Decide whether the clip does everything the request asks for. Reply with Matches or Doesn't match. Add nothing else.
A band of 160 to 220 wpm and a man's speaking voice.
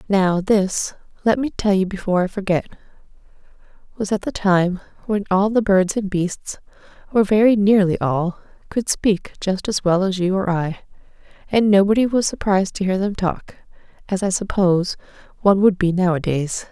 Doesn't match